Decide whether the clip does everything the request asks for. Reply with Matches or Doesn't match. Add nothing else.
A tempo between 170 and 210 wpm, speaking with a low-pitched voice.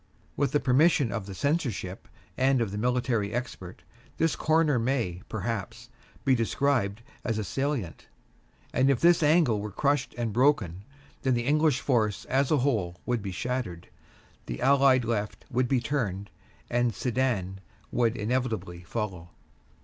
Doesn't match